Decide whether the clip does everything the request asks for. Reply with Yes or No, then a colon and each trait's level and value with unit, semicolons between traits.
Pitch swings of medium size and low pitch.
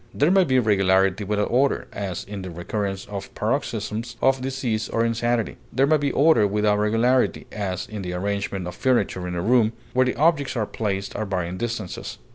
Yes: average, 4.6 semitones; low, 110 Hz